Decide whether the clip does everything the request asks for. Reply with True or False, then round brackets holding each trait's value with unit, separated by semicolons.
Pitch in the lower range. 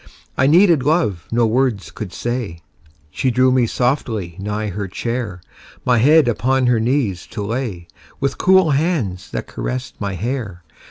True (120 Hz)